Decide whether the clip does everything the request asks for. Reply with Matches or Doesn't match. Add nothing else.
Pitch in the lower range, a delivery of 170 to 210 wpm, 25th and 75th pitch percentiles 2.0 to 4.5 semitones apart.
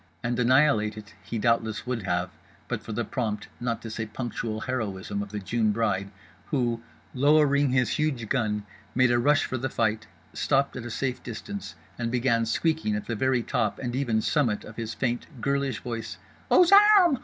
Matches